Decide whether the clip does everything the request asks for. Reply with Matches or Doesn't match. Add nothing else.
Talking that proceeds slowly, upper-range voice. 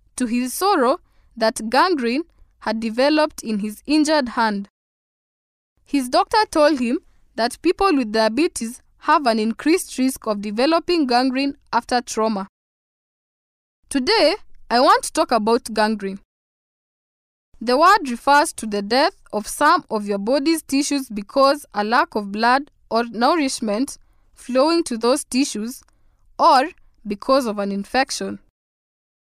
Matches